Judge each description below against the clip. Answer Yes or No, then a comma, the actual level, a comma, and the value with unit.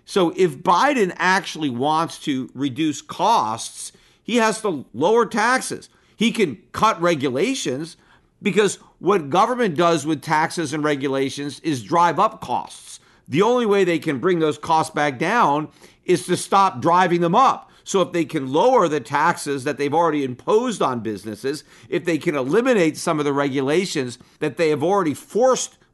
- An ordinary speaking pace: Yes, average, 165 wpm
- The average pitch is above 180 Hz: No, medium, 165 Hz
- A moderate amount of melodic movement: Yes, average, 4.1 semitones